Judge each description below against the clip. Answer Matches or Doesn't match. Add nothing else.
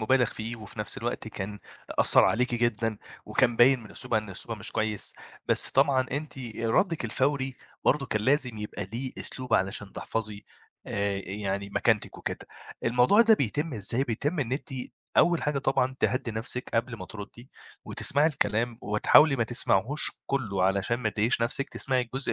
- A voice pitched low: Matches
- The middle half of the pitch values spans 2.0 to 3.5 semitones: Doesn't match